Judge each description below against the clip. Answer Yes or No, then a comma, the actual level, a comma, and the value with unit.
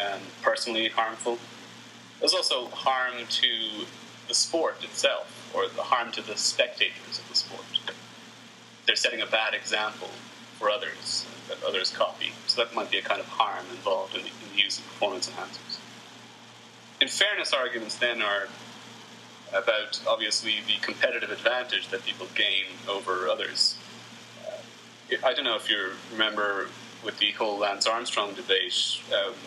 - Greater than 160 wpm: No, average, 155 wpm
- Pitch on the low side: Yes, low, 125 Hz